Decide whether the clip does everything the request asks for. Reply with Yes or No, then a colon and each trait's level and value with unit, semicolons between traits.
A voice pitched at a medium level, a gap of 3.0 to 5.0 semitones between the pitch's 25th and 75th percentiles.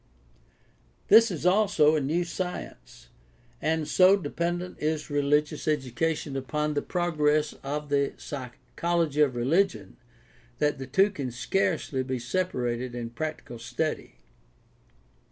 Yes: medium, 150 Hz; average, 4.6 semitones